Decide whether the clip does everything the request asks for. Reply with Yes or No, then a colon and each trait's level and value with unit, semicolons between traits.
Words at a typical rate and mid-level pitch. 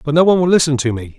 No: fast, 355 wpm; medium, 150 Hz